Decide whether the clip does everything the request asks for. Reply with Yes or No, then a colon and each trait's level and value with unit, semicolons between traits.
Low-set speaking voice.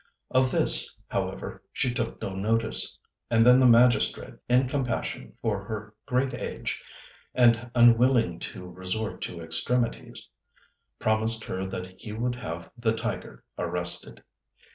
Yes: low, 115 Hz